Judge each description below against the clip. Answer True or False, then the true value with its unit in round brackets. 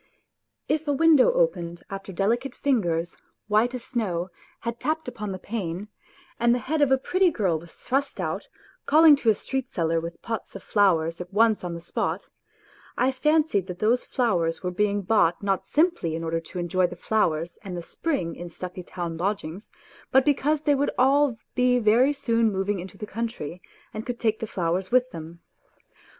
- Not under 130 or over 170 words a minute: False (185 wpm)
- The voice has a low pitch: False (210 Hz)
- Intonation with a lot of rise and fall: True (6.6 semitones)